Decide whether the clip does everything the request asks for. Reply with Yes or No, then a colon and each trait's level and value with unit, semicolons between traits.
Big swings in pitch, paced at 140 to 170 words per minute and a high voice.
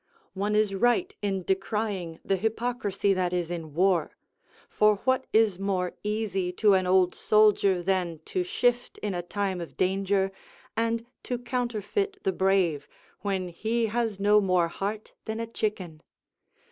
No: average, 3.2 semitones; average, 150 wpm; high, 200 Hz